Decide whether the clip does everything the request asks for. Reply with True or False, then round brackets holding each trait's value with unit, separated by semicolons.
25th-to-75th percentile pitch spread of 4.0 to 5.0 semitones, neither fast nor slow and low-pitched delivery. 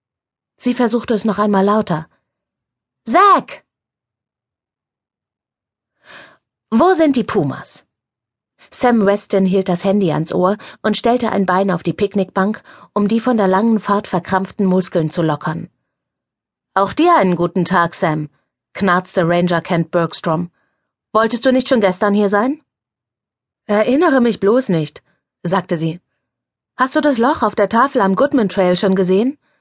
False (4.7 semitones; 140 wpm; 195 Hz)